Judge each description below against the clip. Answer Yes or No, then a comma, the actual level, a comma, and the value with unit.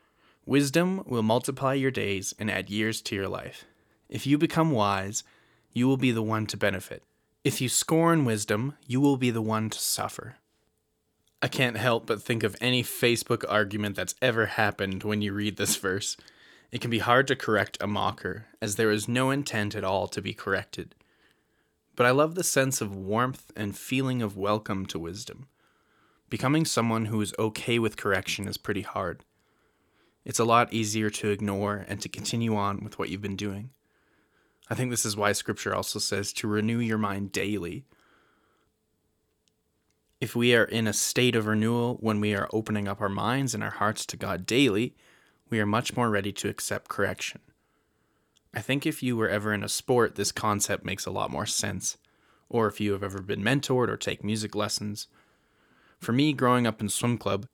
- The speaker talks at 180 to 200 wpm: Yes, average, 190 wpm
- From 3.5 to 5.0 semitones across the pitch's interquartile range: No, average, 3.1 semitones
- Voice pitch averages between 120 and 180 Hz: No, low, 110 Hz